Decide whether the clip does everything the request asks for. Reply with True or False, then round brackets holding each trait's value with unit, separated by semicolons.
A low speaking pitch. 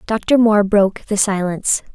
False (205 Hz)